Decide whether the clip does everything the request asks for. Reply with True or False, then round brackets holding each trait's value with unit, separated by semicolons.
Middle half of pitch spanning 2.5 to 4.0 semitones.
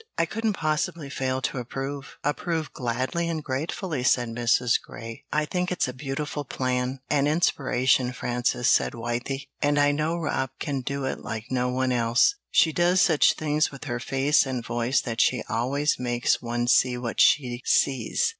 True (3.4 semitones)